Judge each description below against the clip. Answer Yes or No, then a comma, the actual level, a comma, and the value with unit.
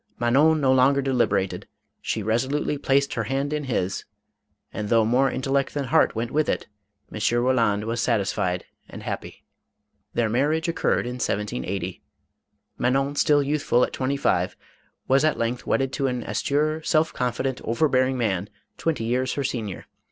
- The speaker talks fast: No, average, 160 wpm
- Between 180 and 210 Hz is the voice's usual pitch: No, low, 130 Hz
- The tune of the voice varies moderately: Yes, average, 3.5 semitones